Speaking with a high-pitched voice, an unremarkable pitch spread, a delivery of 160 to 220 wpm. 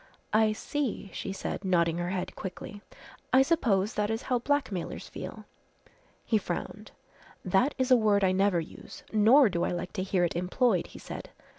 Yes: high, 200 Hz; average, 4.7 semitones; average, 175 wpm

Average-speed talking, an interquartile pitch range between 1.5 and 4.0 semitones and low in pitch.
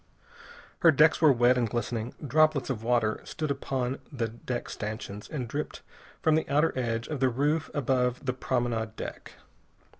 Yes: average, 160 wpm; average, 3.7 semitones; low, 125 Hz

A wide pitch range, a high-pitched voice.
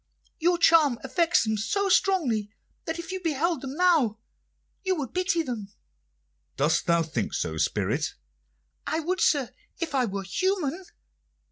Yes: wide, 6.9 semitones; very high, 320 Hz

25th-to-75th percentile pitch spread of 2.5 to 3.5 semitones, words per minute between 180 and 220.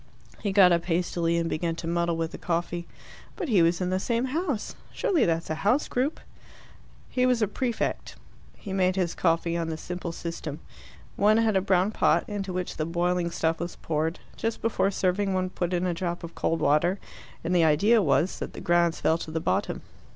Yes: average, 3.2 semitones; fast, 205 wpm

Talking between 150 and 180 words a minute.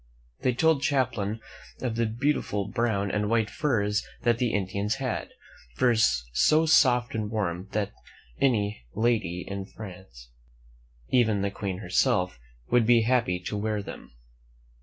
No: average, 140 wpm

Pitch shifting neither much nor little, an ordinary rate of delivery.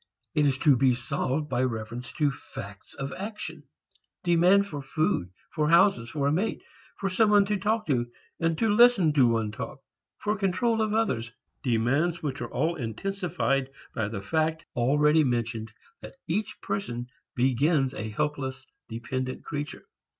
No: wide, 6.6 semitones; average, 155 wpm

